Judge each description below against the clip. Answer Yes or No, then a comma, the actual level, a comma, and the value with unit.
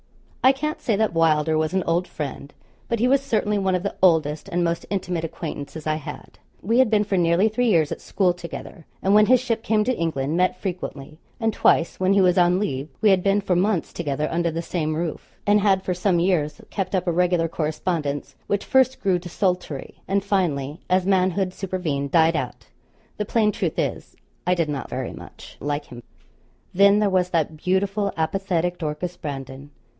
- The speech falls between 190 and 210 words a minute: Yes, average, 200 wpm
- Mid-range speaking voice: Yes, medium, 180 Hz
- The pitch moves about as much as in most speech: Yes, average, 3.9 semitones